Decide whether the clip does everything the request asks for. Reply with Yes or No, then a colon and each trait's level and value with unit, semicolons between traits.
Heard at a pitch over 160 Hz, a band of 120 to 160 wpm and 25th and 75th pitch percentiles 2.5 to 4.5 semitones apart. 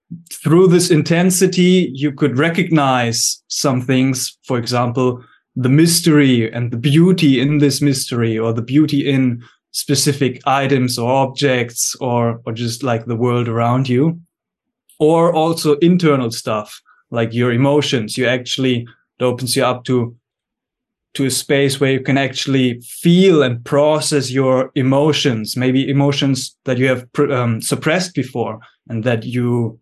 No: low, 130 Hz; average, 145 wpm; average, 3.3 semitones